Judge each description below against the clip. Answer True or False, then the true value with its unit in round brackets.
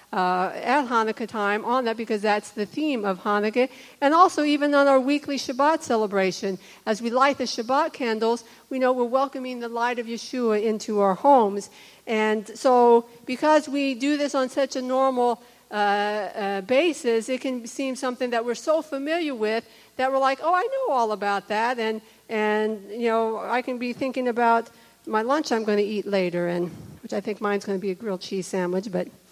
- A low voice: False (235 Hz)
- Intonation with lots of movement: False (4.1 semitones)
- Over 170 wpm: True (200 wpm)